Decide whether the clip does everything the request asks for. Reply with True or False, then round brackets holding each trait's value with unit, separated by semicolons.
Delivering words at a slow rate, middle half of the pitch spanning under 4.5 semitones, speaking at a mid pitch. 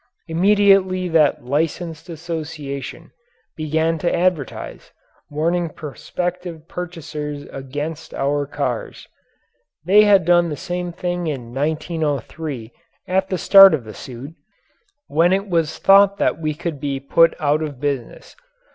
True (125 wpm; 3.5 semitones; 160 Hz)